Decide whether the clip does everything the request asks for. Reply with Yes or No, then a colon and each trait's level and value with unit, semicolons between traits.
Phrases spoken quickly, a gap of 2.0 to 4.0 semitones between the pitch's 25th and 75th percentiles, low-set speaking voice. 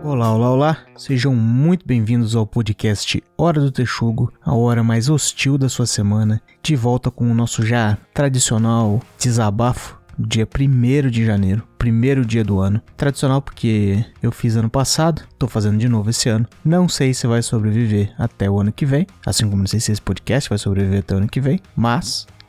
Yes: fast, 190 wpm; average, 3.5 semitones; low, 115 Hz